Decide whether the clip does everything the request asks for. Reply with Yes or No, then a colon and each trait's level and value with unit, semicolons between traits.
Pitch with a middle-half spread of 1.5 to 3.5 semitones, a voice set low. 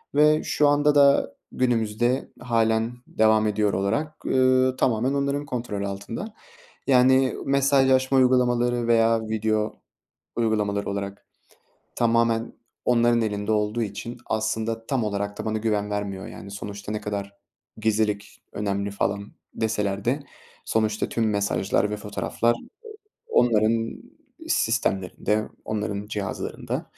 Yes: average, 3.1 semitones; low, 110 Hz